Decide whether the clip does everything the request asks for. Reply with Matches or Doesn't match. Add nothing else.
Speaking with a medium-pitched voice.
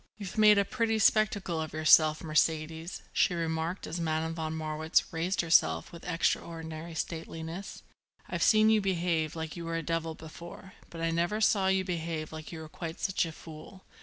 Matches